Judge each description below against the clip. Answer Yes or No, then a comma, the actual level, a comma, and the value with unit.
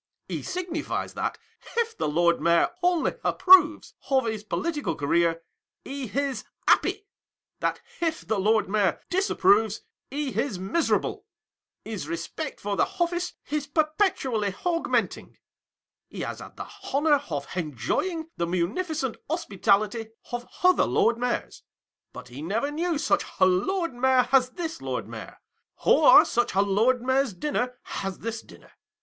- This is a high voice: Yes, very high, 250 Hz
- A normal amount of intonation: No, wide, 8.4 semitones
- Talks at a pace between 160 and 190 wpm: No, average, 145 wpm